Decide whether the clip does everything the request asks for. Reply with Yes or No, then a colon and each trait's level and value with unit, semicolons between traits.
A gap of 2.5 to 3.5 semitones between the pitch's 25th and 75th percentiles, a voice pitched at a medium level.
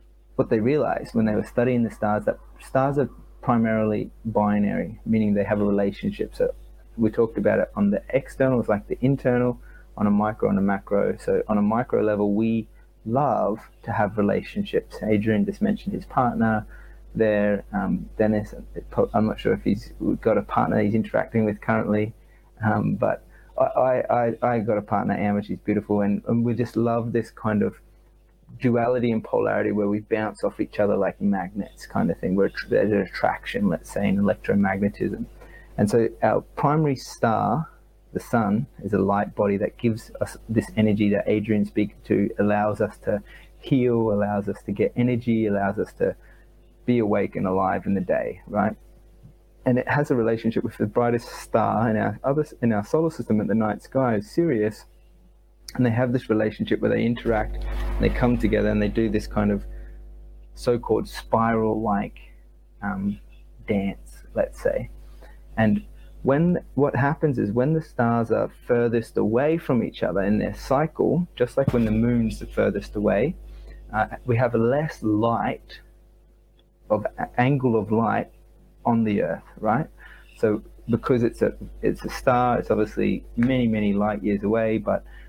No: average, 2.9 semitones; low, 110 Hz